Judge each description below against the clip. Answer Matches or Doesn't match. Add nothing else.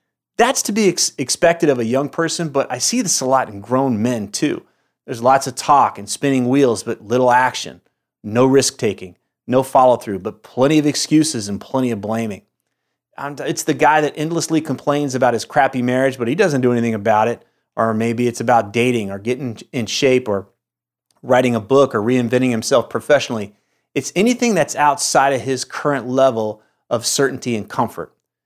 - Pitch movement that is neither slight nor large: Matches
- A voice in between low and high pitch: Doesn't match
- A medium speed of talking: Matches